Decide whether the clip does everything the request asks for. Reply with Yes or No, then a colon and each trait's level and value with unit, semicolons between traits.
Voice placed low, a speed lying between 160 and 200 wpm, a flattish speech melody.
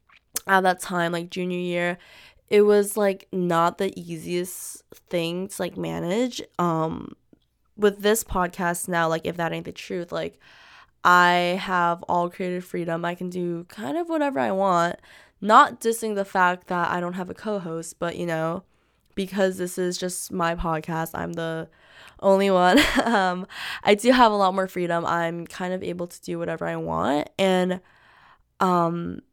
No: medium, 180 Hz; average, 170 wpm; narrow, 2.0 semitones